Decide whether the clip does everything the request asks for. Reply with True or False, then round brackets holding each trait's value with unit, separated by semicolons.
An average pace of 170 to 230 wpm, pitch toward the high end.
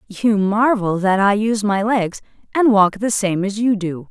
True (205 wpm; 205 Hz)